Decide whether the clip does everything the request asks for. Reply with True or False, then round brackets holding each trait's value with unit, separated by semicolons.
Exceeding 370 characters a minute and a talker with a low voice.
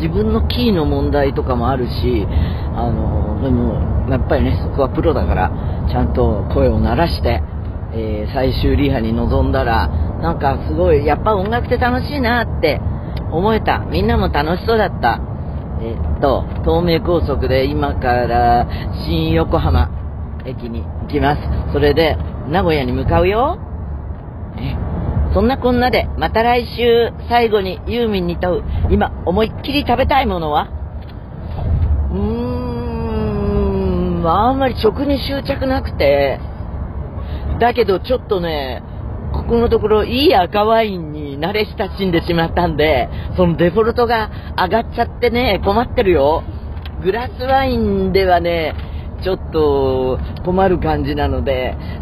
False (275 characters per minute; 110 Hz)